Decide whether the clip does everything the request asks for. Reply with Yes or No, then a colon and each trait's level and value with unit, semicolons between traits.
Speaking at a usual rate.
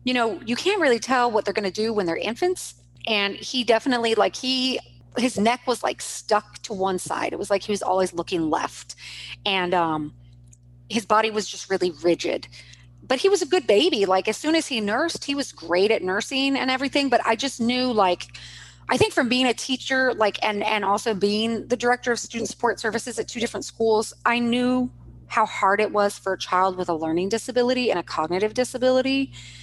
No: fast, 215 wpm